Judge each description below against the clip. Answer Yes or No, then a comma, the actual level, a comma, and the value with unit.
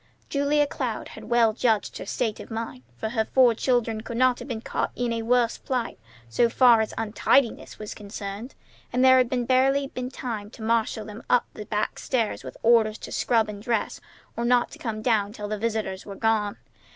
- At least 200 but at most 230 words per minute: Yes, fast, 205 wpm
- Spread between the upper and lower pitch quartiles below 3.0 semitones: Yes, narrow, 2.4 semitones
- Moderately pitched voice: No, high, 230 Hz